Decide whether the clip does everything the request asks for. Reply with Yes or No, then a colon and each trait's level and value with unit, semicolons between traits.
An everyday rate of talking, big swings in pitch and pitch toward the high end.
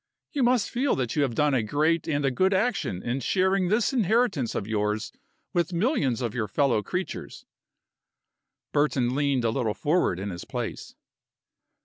No: average, 165 wpm; wide, 8.1 semitones; medium, 145 Hz